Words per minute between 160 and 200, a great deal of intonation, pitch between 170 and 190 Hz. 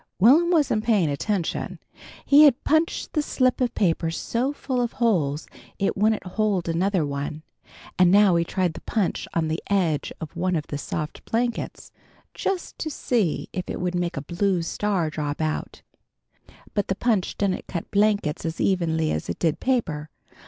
Yes: average, 175 wpm; wide, 5.7 semitones; medium, 185 Hz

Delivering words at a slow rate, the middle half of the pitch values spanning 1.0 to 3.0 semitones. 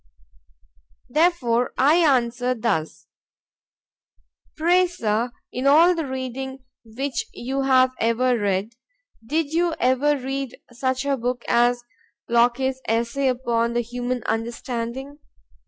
Yes: slow, 110 wpm; average, 2.7 semitones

